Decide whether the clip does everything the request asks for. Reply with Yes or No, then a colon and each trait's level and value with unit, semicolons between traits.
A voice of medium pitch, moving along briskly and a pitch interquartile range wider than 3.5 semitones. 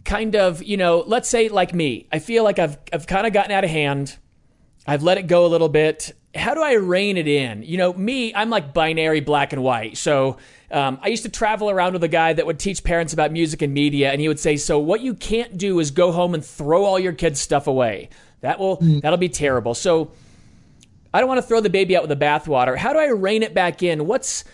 Yes: medium, 170 Hz; fast, 250 wpm; average, 4.7 semitones